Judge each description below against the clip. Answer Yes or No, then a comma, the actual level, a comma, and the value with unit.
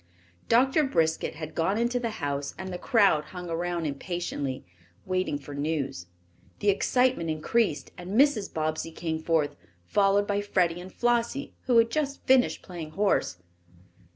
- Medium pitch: Yes, medium, 180 Hz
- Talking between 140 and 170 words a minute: Yes, average, 150 wpm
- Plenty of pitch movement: Yes, wide, 6.6 semitones